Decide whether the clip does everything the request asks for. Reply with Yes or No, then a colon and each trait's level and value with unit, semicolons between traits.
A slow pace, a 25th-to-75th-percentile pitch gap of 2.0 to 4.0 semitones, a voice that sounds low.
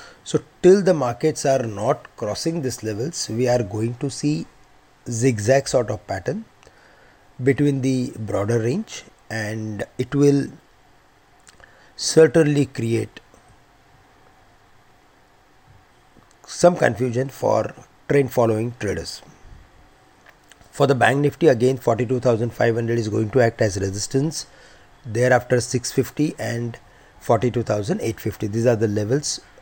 Yes: slow, 115 wpm; average, 3.7 semitones; low, 125 Hz